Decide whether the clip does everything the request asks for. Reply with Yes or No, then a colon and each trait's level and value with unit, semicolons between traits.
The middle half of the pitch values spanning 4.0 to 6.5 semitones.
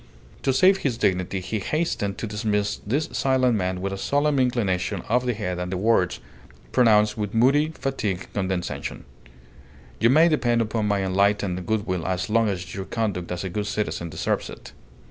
Yes: average, 4.4 semitones